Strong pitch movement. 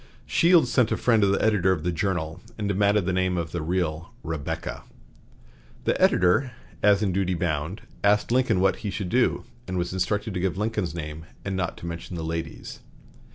No: average, 3.4 semitones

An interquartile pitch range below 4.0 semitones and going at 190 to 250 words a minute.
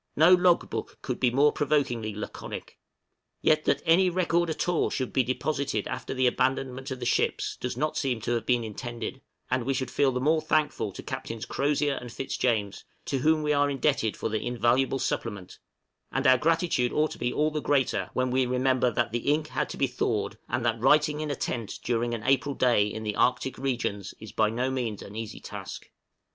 Yes: average, 3.6 semitones; fast, 205 wpm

